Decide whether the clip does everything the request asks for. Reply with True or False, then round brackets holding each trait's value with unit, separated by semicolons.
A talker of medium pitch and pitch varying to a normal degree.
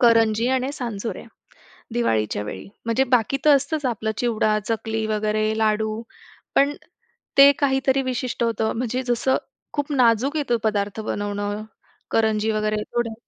False (230 Hz; 3.2 semitones)